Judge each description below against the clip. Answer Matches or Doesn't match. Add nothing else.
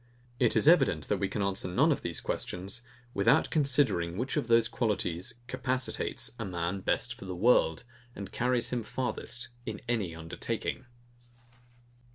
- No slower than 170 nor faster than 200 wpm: Doesn't match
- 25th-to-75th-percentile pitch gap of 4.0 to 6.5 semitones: Matches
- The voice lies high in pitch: Doesn't match